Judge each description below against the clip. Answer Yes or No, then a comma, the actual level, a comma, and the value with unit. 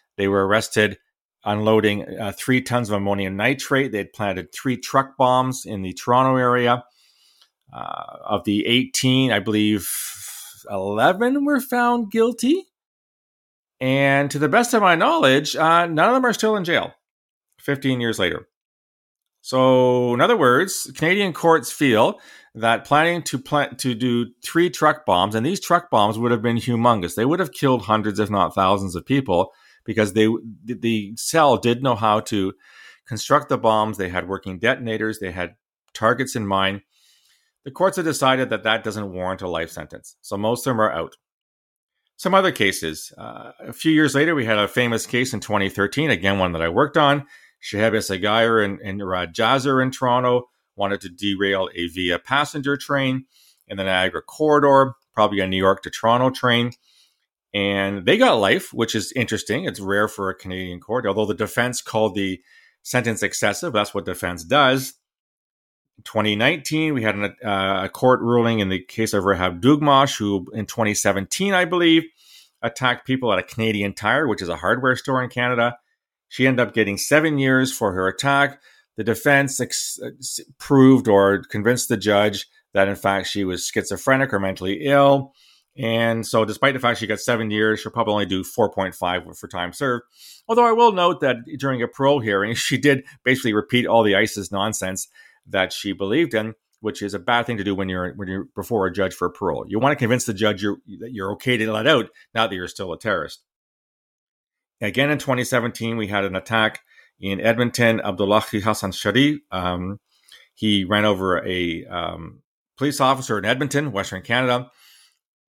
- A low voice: Yes, low, 115 Hz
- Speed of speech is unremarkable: Yes, average, 180 wpm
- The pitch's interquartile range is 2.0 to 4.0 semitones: No, average, 4.8 semitones